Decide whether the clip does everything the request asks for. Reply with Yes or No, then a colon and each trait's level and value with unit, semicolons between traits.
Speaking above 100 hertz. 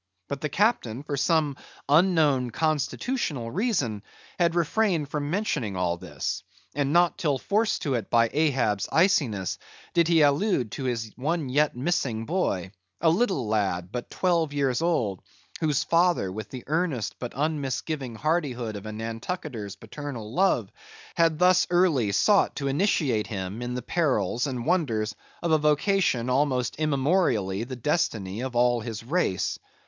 Yes: medium, 140 Hz